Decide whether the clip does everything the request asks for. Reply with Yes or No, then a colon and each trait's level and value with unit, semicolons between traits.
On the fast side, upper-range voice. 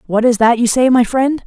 Yes: fast, 285 wpm; high, 240 Hz